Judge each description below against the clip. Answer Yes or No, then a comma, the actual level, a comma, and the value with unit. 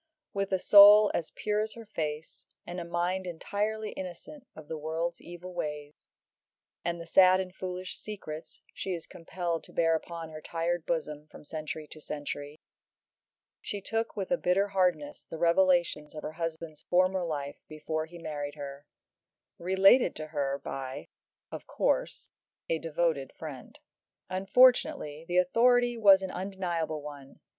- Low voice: No, medium, 170 Hz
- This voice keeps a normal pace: Yes, average, 150 wpm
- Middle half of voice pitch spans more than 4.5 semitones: No, average, 3.6 semitones